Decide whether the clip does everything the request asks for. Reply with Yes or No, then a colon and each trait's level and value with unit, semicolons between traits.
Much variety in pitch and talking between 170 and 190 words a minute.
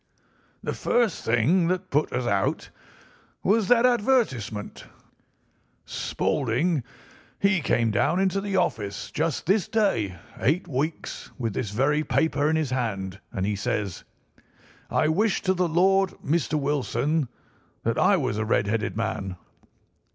No: wide, 8.6 semitones; slow, 135 wpm